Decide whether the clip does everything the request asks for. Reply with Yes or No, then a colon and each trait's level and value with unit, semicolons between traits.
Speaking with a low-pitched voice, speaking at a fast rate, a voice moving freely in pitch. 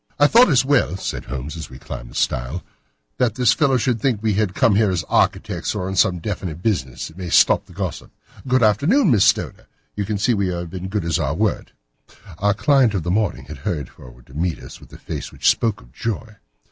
Yes: low, 100 Hz; fast, 235 wpm; wide, 5.7 semitones